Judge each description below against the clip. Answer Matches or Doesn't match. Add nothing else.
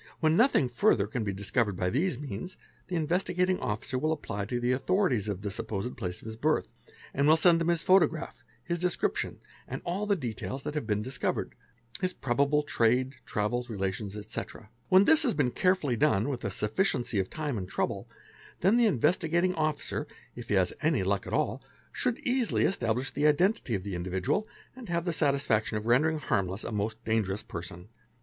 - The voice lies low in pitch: Matches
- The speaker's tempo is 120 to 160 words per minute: Doesn't match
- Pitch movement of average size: Doesn't match